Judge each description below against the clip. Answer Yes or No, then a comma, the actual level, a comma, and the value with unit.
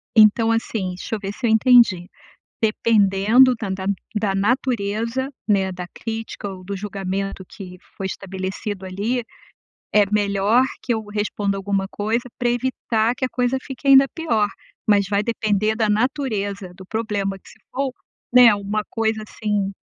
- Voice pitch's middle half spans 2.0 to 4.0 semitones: Yes, average, 2.9 semitones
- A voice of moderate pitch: No, high, 210 Hz